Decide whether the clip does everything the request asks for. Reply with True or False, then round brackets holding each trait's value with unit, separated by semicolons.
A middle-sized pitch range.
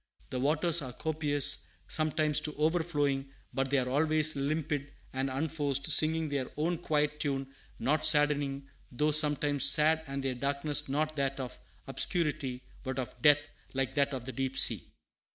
False (2.2 semitones)